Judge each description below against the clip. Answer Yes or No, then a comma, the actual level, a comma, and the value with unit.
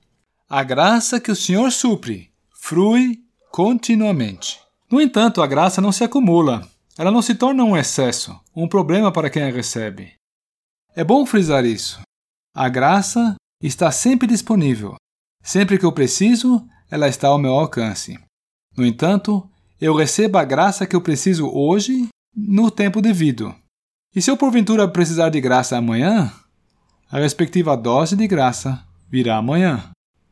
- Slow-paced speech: No, average, 145 wpm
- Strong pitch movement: Yes, wide, 8.7 semitones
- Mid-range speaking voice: Yes, medium, 175 Hz